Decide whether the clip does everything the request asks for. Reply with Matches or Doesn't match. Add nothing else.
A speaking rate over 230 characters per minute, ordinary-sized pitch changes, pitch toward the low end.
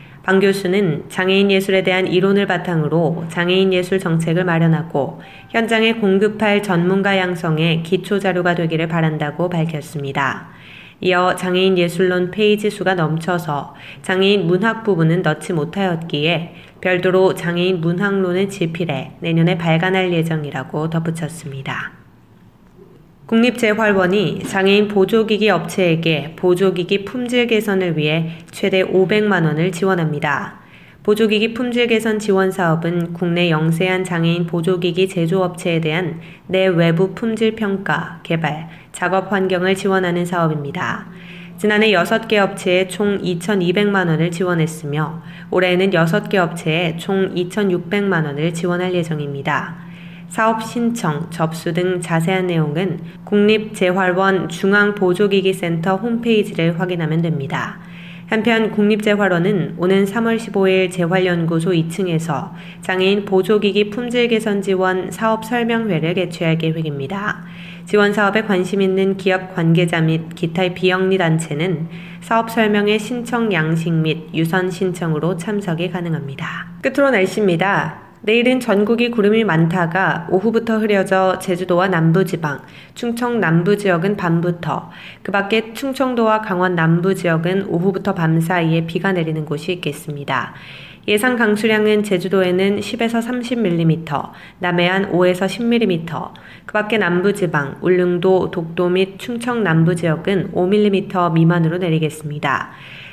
Doesn't match